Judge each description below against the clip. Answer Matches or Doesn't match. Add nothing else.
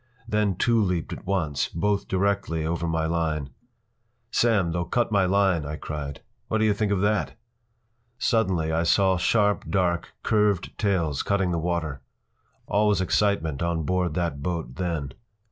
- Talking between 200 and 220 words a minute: Doesn't match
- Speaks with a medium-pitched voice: Doesn't match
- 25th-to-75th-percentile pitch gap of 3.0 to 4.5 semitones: Matches